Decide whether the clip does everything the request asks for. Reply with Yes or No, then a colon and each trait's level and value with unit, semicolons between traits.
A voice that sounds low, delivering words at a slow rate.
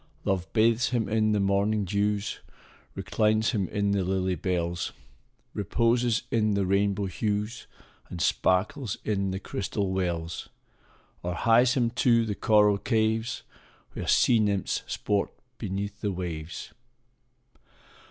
Yes: low, 100 Hz; slow, 125 wpm